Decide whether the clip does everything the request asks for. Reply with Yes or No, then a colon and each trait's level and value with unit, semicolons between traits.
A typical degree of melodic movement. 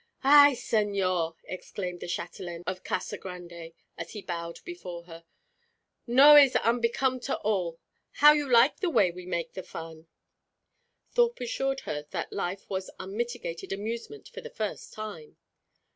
No: wide, 7.1 semitones